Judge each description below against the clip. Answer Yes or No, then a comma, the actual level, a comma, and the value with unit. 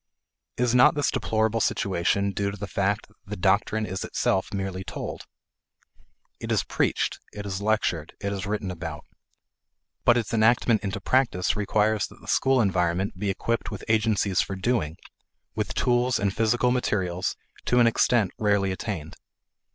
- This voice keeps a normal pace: Yes, average, 160 wpm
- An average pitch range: Yes, average, 3.0 semitones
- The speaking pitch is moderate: No, low, 105 Hz